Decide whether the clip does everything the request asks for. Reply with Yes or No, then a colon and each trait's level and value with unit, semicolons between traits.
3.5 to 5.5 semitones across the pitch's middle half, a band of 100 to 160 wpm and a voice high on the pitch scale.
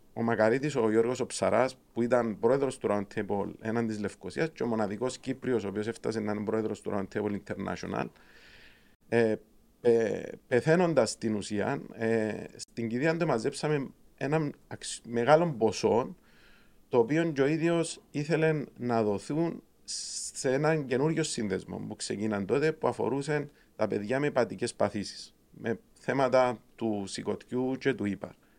No: average, 5.2 semitones; average, 145 wpm; low, 120 Hz